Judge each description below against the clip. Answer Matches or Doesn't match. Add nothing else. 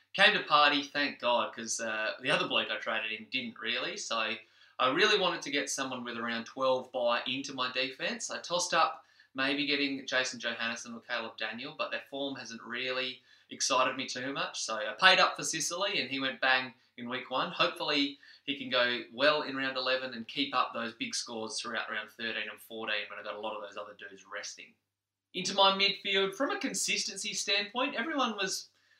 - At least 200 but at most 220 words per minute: Matches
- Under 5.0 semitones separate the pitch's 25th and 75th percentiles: Doesn't match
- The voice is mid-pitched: Doesn't match